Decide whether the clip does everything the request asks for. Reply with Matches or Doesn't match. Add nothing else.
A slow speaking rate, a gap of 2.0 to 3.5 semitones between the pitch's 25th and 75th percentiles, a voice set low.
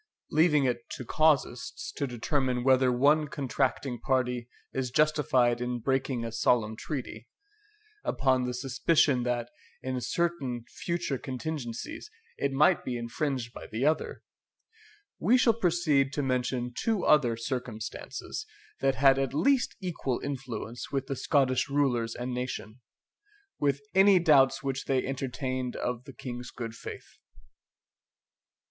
Matches